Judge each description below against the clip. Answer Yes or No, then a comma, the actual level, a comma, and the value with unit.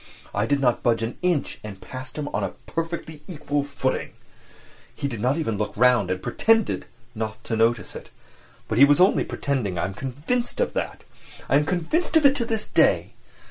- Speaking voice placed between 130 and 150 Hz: Yes, medium, 140 Hz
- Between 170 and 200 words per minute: Yes, average, 195 wpm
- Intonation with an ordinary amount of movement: No, wide, 6.7 semitones